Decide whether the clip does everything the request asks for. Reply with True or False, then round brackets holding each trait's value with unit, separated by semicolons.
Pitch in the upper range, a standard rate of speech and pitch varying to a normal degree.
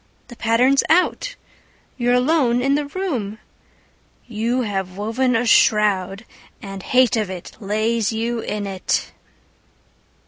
False (230 Hz; 125 wpm; 3.5 semitones)